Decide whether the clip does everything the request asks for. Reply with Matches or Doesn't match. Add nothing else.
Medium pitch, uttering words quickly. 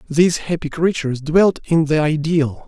Doesn't match